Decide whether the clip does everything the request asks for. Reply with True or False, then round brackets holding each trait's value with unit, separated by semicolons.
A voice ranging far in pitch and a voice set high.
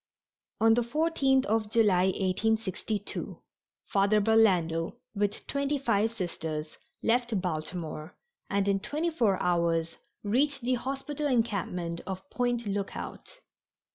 False (4.9 semitones; 210 Hz)